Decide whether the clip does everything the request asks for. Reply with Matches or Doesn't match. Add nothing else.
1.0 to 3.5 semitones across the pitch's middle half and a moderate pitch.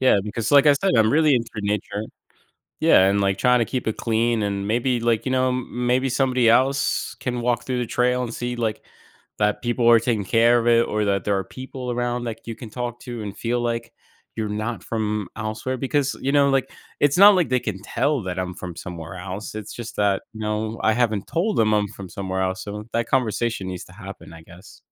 Doesn't match